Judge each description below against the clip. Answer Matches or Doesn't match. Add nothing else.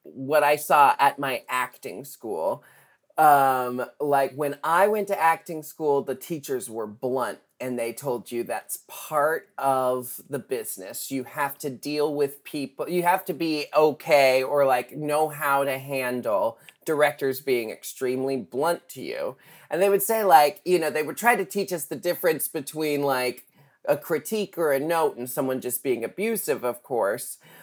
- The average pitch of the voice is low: Doesn't match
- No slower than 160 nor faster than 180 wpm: Matches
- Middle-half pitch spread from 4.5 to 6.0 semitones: Doesn't match